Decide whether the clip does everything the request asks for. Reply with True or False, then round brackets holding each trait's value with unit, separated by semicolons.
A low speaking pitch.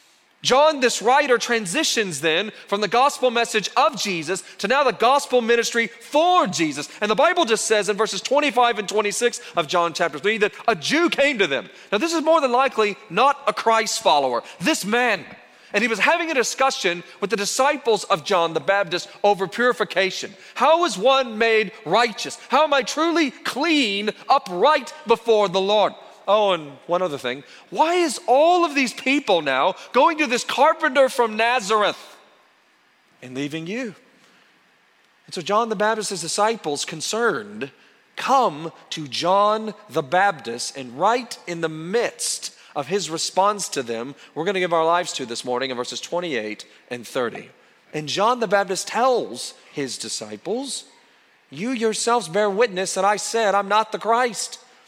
False (215 Hz)